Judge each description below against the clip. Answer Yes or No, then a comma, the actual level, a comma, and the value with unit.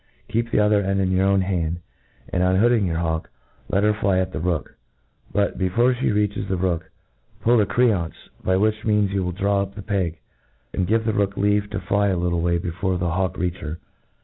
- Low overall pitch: Yes, very low, 95 Hz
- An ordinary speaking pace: No, fast, 215 wpm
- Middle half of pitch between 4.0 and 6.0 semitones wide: No, average, 2.7 semitones